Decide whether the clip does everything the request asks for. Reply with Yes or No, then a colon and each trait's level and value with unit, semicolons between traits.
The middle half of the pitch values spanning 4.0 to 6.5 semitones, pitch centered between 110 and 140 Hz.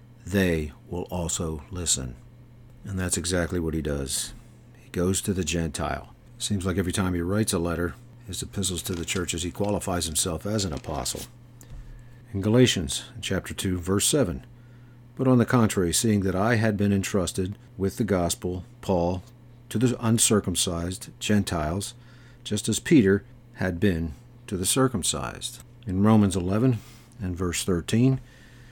No: average, 5.0 semitones; low, 100 Hz